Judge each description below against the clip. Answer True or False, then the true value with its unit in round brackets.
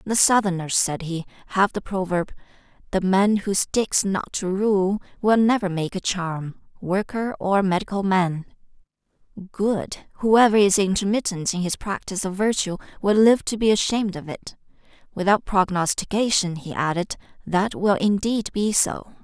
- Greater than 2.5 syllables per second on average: True (4.7 syllables/s)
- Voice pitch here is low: False (195 Hz)